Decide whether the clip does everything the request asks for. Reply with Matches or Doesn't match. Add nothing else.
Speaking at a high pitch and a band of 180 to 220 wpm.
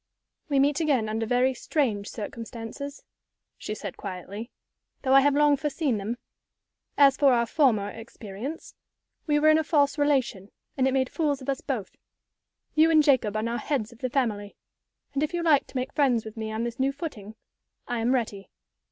Matches